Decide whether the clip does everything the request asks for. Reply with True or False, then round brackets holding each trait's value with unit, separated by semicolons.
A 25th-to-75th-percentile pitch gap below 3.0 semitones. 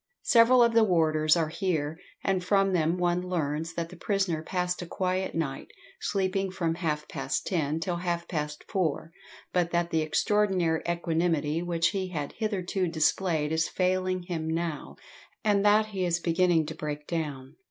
True (2.6 semitones)